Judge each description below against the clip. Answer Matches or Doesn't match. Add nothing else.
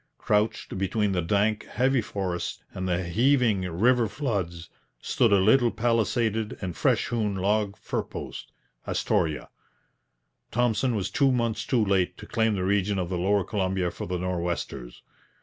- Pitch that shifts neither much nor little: Matches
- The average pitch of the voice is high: Doesn't match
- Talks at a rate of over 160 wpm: Doesn't match